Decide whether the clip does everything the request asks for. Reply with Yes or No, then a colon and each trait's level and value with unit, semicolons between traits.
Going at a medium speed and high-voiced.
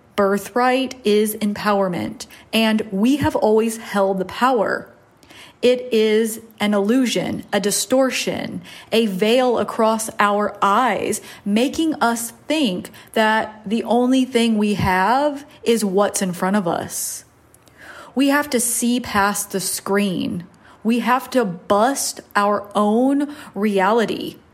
No: slow, 120 wpm; high, 220 Hz